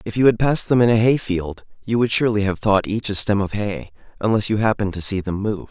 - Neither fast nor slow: No, fast, 275 wpm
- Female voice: No, male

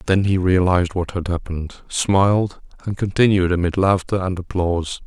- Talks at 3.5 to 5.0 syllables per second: No, 5.2 syllables/s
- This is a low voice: Yes, very low, 90 Hz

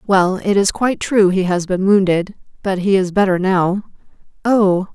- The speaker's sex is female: Yes, female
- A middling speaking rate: Yes, average, 180 wpm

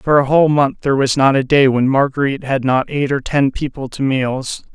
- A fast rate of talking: Yes, fast, 240 wpm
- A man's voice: Yes, male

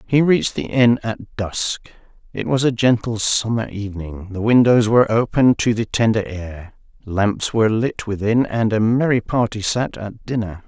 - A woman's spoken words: No, male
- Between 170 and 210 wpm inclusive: Yes, average, 175 wpm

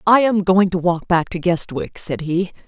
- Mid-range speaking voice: Yes, medium, 180 Hz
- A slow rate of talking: No, fast, 225 wpm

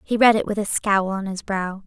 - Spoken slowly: No, fast, 290 wpm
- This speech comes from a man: No, female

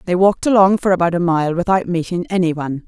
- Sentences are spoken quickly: Yes, fast, 210 wpm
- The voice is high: No, medium, 180 Hz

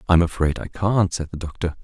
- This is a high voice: No, very low, 85 Hz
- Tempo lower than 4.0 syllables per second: No, 6.5 syllables/s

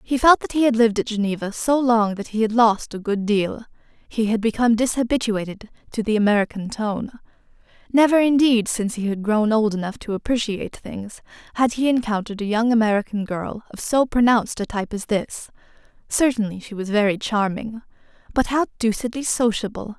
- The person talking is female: Yes, female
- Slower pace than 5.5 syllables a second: No, 5.6 syllables/s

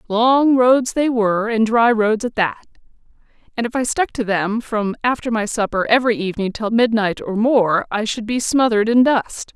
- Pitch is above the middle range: Yes, high, 225 Hz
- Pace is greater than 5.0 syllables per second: No, 4.9 syllables/s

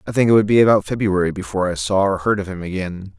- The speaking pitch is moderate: No, very low, 95 Hz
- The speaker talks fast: Yes, fast, 285 wpm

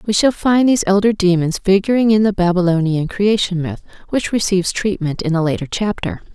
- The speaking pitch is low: No, high, 190 Hz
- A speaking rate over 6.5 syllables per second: No, 5.7 syllables/s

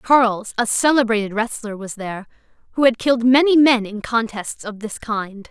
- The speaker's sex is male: No, female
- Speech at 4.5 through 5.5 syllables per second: Yes, 5.2 syllables/s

